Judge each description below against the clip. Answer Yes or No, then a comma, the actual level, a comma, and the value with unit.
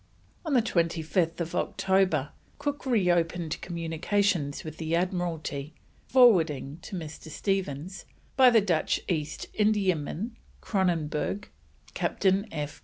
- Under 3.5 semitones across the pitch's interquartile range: No, average, 4.0 semitones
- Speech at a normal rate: No, slow, 100 wpm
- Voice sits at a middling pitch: Yes, medium, 175 Hz